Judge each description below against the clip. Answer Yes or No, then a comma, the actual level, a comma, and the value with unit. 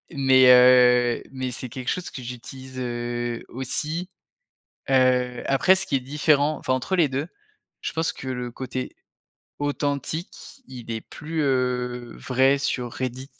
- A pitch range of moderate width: No, narrow, 2.3 semitones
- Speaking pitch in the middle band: No, low, 130 Hz